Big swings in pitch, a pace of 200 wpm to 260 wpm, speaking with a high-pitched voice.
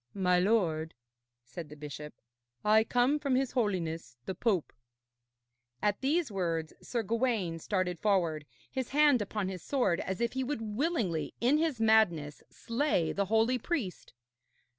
No: wide, 6.4 semitones; average, 145 wpm; high, 210 Hz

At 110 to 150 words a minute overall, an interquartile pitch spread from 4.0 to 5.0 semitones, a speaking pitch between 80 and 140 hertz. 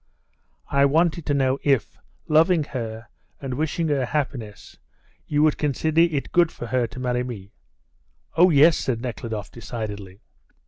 Yes: average, 145 wpm; average, 4.7 semitones; low, 135 Hz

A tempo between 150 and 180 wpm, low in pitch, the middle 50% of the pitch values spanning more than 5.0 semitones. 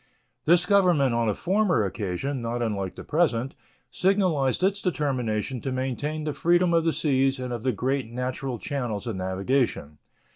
Yes: average, 160 wpm; low, 130 Hz; wide, 5.6 semitones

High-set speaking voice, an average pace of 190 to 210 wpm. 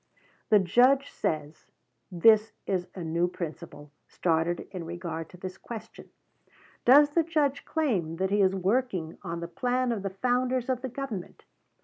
No: high, 195 Hz; average, 155 wpm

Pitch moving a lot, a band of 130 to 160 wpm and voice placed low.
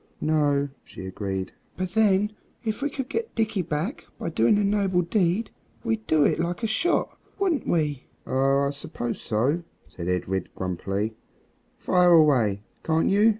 No: wide, 8.8 semitones; average, 155 wpm; medium, 165 Hz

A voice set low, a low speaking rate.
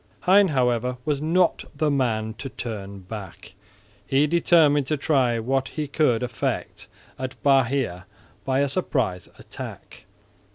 Yes: low, 130 Hz; slow, 130 wpm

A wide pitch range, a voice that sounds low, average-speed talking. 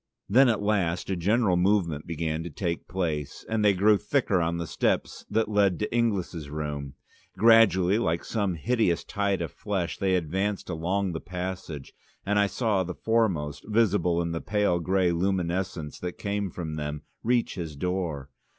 No: average, 3.6 semitones; very low, 90 Hz; average, 170 wpm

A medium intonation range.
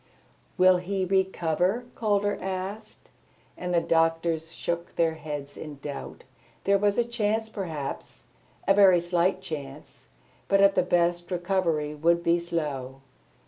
Yes: average, 3.2 semitones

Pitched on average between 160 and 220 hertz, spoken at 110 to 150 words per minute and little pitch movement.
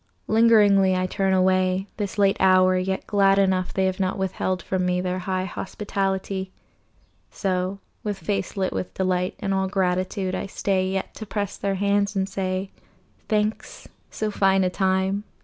No: high, 190 Hz; average, 165 wpm; narrow, 1.1 semitones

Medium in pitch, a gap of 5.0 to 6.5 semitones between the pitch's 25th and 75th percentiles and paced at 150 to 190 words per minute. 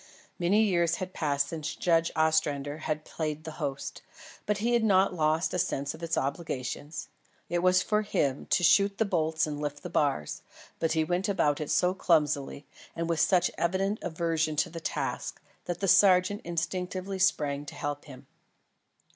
No: medium, 165 Hz; average, 3.5 semitones; average, 175 wpm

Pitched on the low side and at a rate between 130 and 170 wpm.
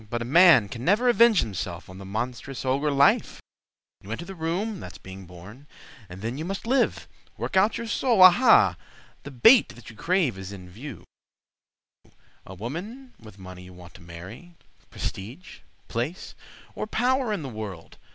Yes: low, 130 Hz; average, 165 wpm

